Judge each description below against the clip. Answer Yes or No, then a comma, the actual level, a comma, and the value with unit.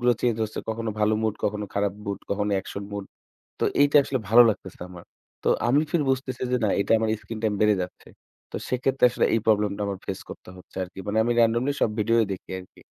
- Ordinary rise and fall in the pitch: Yes, average, 3.1 semitones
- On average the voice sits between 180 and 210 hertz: No, low, 110 Hz